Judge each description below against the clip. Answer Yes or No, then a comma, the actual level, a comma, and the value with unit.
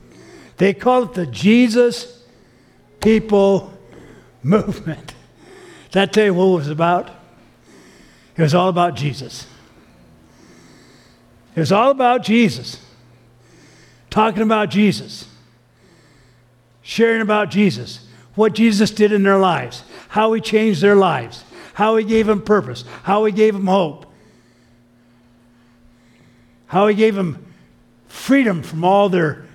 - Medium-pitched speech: Yes, medium, 180 Hz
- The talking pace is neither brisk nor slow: No, slow, 120 wpm